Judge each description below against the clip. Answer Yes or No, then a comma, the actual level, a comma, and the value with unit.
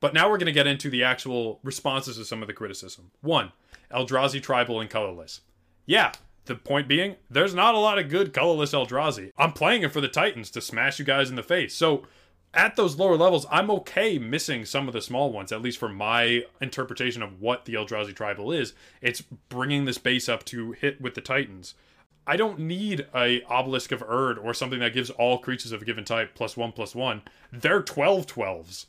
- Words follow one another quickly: Yes, fast, 215 wpm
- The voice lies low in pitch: Yes, low, 125 Hz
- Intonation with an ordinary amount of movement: Yes, average, 3.7 semitones